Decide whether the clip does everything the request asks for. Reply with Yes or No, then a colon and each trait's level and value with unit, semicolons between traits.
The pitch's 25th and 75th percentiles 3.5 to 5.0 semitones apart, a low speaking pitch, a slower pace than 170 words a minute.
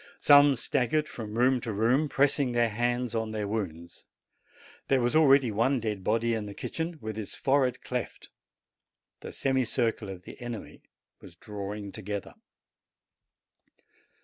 Yes: average, 3.9 semitones; low, 115 Hz; average, 145 wpm